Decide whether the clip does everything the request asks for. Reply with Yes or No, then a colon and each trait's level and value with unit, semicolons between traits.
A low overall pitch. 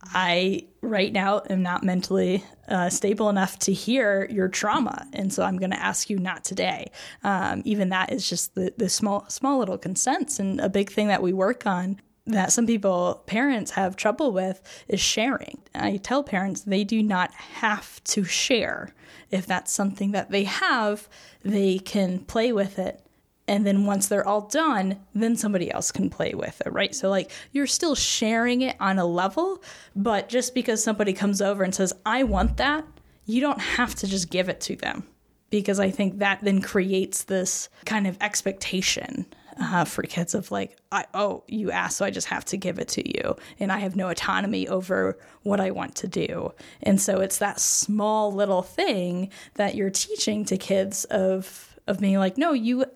No: high, 200 Hz